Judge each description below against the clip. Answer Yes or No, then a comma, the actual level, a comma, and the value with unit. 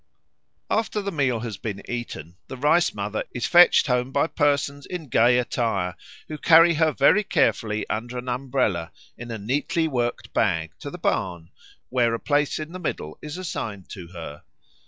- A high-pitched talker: No, low, 125 Hz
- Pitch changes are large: Yes, wide, 5.9 semitones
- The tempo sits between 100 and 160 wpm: No, average, 175 wpm